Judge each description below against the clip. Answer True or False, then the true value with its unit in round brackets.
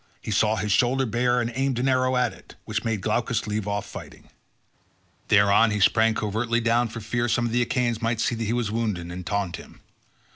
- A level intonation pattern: True (2.3 semitones)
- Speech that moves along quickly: True (215 wpm)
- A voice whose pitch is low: True (115 Hz)